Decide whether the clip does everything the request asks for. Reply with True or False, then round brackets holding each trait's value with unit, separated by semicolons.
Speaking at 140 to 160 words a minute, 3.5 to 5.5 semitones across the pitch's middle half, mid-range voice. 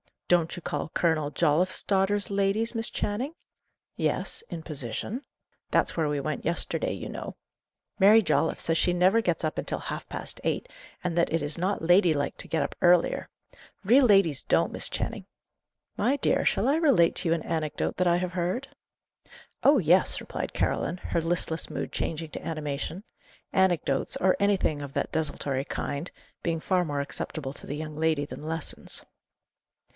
False (170 wpm; 4.1 semitones; 170 Hz)